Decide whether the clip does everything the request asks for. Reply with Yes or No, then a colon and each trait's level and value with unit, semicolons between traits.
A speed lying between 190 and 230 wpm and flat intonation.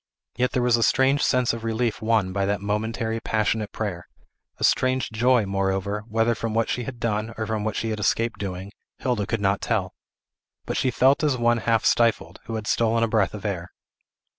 Yes: fast, 205 wpm; narrow, 2.3 semitones